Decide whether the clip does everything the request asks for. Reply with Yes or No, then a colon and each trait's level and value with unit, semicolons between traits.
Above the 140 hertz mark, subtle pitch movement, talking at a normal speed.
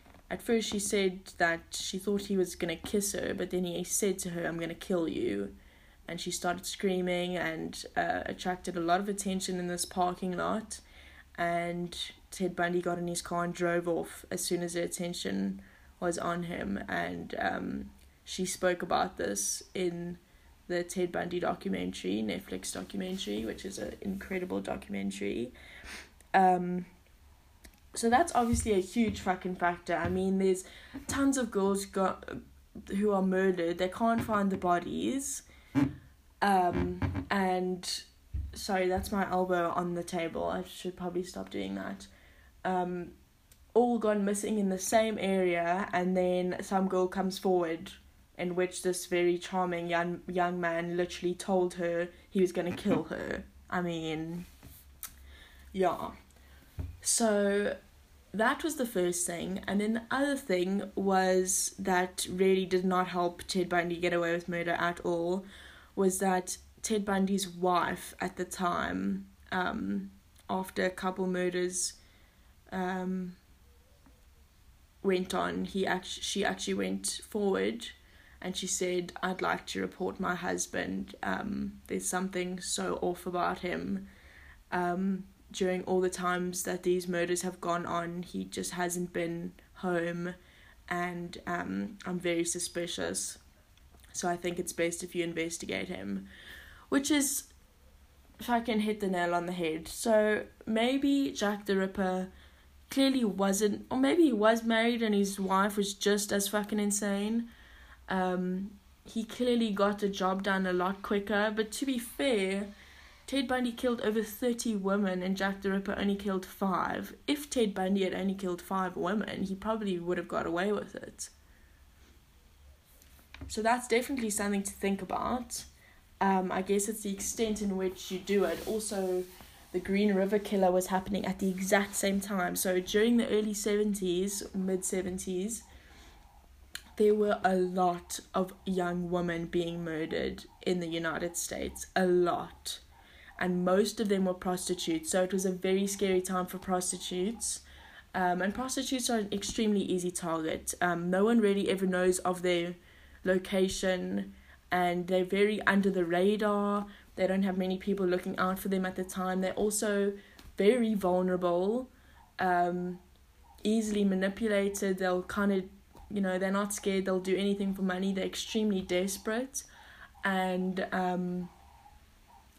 Yes: medium, 185 Hz; narrow, 2.3 semitones; average, 155 wpm